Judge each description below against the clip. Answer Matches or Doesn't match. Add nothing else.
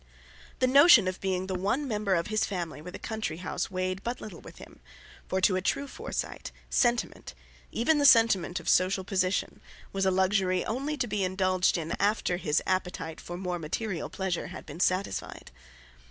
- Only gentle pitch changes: Doesn't match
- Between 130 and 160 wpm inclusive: Doesn't match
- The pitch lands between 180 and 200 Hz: Matches